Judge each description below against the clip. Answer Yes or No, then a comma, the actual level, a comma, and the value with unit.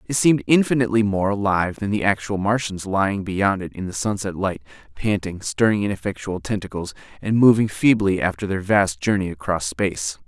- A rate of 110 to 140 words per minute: No, average, 170 wpm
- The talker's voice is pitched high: No, very low, 95 Hz